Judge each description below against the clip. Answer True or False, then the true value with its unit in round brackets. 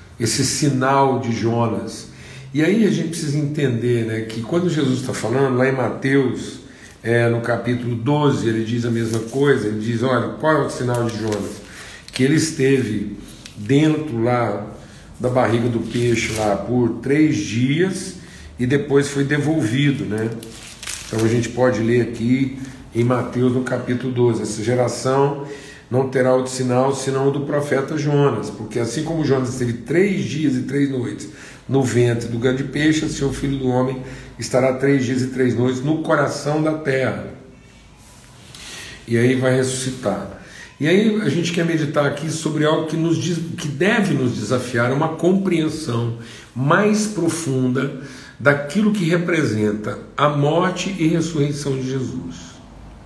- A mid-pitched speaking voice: False (130 Hz)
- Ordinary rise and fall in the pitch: True (3.8 semitones)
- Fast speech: False (160 wpm)